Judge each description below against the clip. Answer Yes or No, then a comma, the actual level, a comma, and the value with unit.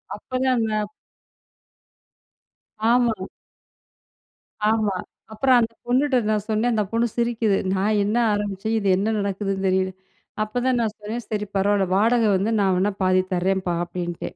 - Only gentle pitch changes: No, average, 3.0 semitones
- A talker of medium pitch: No, high, 210 Hz